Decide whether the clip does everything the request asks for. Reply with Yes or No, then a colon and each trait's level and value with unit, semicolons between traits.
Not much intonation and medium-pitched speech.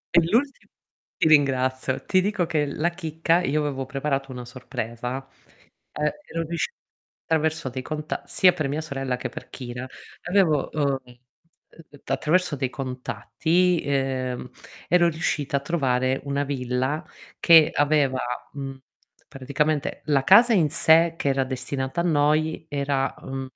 No: average, 3.4 semitones; medium, 145 Hz